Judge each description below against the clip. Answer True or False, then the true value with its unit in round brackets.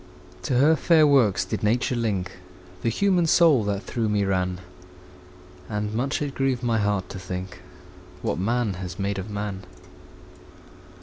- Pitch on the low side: True (105 Hz)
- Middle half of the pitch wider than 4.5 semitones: True (4.9 semitones)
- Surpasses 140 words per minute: True (150 wpm)